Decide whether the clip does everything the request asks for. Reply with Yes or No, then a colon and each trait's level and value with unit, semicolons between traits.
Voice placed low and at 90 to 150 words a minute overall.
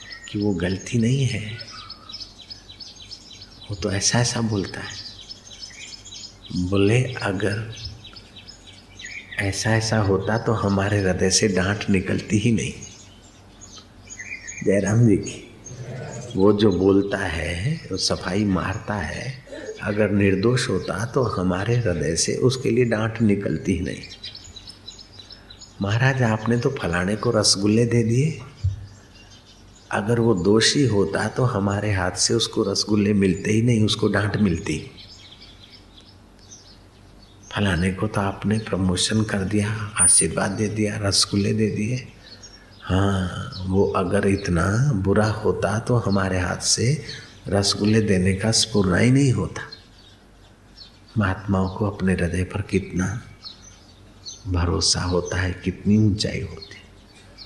Yes: low, 100 Hz; average, 120 wpm